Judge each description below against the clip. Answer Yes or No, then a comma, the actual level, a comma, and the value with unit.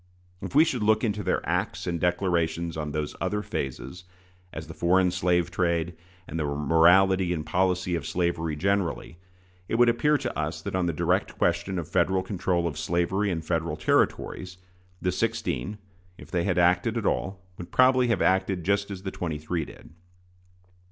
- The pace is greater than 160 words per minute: Yes, average, 180 wpm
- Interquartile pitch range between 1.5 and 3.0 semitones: Yes, average, 2.7 semitones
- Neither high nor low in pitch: No, very low, 90 Hz